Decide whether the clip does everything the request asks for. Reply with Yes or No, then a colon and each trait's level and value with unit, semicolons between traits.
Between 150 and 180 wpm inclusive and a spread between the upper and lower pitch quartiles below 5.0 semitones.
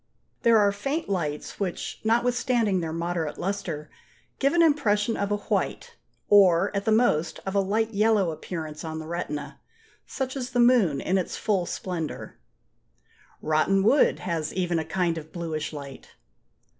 No: average, 155 wpm; average, 5.3 semitones